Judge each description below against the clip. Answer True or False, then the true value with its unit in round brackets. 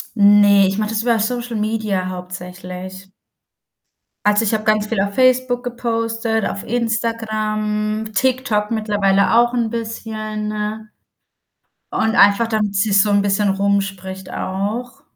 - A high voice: True (215 Hz)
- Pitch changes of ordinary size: False (2.2 semitones)